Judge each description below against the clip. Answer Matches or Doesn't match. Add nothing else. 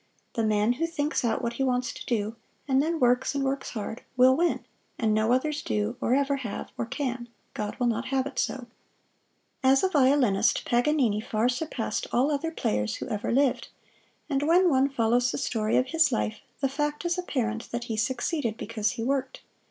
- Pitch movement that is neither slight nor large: Matches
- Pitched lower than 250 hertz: Doesn't match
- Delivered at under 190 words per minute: Doesn't match